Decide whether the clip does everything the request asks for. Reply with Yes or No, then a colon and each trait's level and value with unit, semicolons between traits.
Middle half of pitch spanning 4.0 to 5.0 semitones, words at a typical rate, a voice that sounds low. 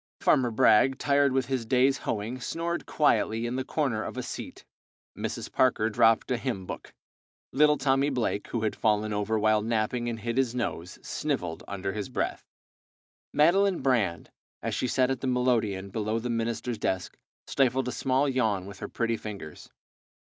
No: average, 3.6 semitones; average, 170 wpm; low, 120 Hz